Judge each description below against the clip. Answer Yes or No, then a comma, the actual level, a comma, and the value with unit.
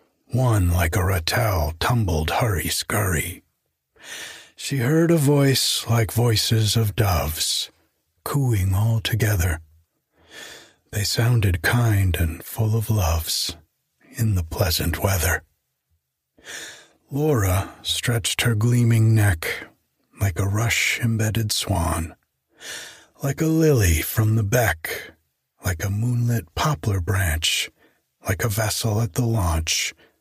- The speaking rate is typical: No, slow, 110 wpm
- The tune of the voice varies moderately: Yes, average, 5.0 semitones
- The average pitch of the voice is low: Yes, low, 105 Hz